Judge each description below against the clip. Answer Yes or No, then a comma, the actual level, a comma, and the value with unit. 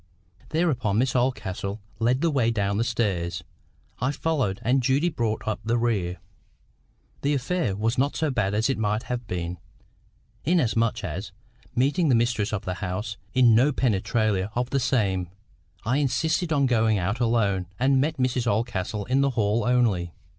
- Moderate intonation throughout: Yes, average, 4.4 semitones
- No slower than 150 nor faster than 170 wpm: Yes, average, 165 wpm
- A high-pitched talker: No, low, 115 Hz